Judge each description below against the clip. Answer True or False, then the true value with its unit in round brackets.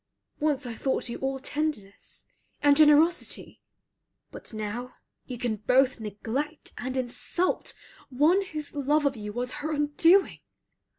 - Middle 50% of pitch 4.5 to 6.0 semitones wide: False (3.7 semitones)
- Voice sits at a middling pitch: False (270 Hz)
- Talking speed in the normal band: False (130 wpm)